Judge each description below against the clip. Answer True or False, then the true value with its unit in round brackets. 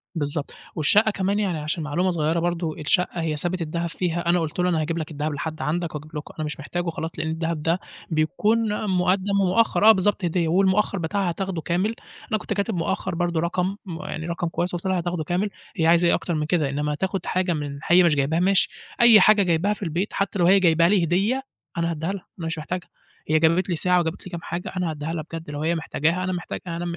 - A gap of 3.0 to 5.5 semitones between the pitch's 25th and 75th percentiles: False (2.6 semitones)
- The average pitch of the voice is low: False (170 Hz)